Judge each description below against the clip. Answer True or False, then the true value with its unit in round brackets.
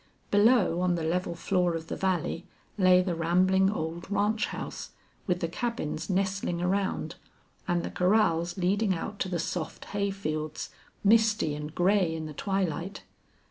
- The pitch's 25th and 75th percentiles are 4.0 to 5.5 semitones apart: False (2.9 semitones)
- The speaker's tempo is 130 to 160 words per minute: True (155 wpm)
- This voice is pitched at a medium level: True (180 Hz)